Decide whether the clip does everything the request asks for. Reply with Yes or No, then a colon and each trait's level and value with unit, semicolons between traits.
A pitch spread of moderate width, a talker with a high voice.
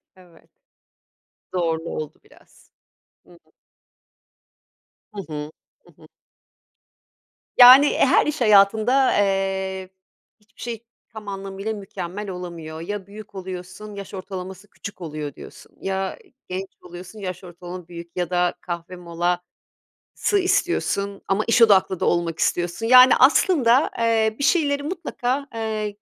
Yes: average, 3.7 semitones; high, 195 Hz